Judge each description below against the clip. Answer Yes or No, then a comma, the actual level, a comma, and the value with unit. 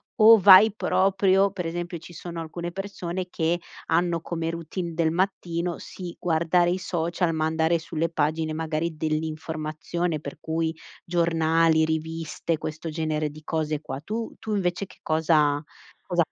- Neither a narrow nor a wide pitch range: No, narrow, 1.9 semitones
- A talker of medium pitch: Yes, medium, 165 Hz